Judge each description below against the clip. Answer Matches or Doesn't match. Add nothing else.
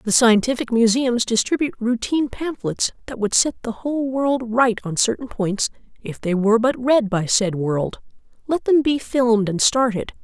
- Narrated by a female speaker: Matches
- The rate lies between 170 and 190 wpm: Matches